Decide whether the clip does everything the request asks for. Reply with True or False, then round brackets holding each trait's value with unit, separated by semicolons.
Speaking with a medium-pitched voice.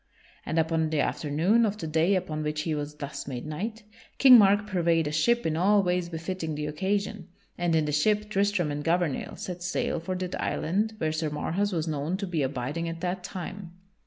True (170 Hz)